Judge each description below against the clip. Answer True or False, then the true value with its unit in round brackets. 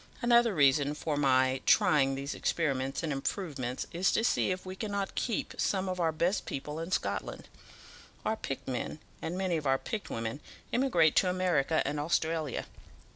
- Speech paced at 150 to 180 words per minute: True (170 wpm)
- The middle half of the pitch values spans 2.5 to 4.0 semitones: False (5.3 semitones)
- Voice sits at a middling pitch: True (160 Hz)